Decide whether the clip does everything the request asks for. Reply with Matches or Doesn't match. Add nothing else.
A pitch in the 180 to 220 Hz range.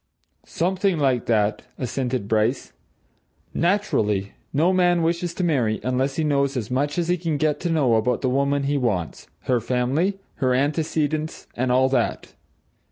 Doesn't match